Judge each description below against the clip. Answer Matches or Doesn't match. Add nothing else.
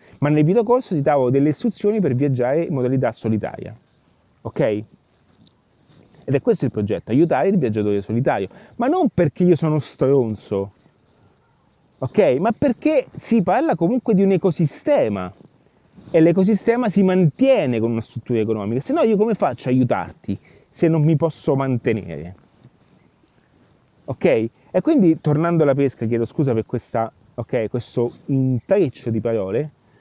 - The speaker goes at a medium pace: Matches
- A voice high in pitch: Doesn't match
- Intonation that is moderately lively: Doesn't match